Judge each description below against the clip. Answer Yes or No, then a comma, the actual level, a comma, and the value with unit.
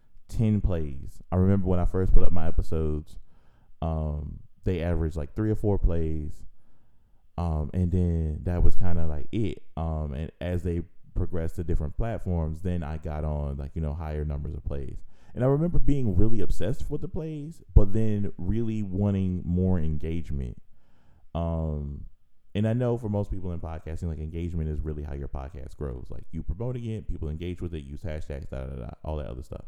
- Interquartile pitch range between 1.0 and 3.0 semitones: No, average, 4.4 semitones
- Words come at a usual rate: Yes, average, 190 wpm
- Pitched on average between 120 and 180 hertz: No, very low, 85 Hz